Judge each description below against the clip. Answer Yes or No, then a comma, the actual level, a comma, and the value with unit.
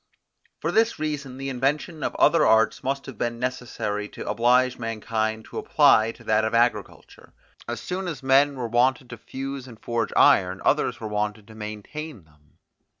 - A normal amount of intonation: Yes, average, 3.7 semitones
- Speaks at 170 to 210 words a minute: Yes, average, 175 wpm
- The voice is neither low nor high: No, low, 120 Hz